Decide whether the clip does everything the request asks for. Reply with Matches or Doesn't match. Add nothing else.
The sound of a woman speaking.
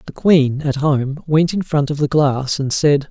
Doesn't match